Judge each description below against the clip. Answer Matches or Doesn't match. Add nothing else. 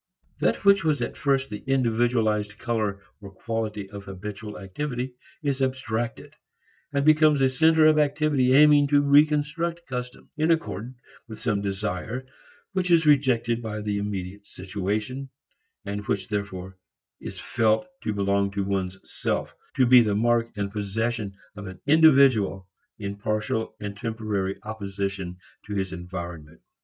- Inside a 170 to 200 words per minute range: Doesn't match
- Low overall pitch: Matches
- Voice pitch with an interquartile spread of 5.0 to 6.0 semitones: Matches